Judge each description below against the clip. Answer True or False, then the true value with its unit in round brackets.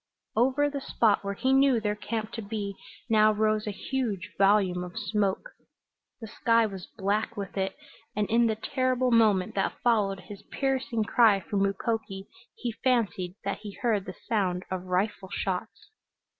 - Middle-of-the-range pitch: False (210 Hz)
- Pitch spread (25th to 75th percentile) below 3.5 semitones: True (2.9 semitones)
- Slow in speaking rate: False (165 wpm)